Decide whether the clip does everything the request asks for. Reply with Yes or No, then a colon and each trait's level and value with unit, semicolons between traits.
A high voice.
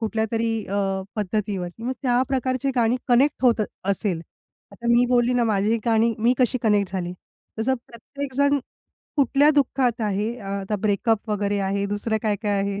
Yes: high, 225 Hz